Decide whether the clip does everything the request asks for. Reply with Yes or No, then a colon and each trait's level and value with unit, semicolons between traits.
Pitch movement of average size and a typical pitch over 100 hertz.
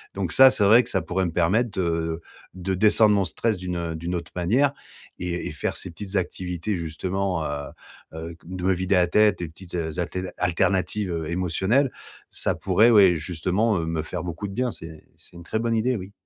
No: average, 3.5 semitones; very low, 90 Hz